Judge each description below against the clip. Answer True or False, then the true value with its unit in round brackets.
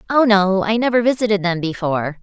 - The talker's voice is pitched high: True (200 Hz)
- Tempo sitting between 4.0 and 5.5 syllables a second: False (6.0 syllables/s)